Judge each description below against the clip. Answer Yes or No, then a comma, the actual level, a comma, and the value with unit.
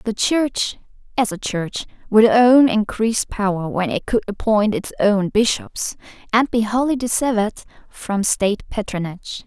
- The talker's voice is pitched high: Yes, high, 220 Hz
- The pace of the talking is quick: No, average, 145 wpm